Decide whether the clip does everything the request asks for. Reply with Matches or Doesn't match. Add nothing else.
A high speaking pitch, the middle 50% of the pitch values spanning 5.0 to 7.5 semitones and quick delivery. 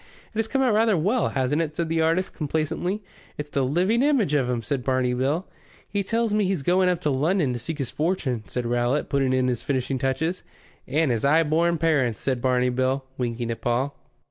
Doesn't match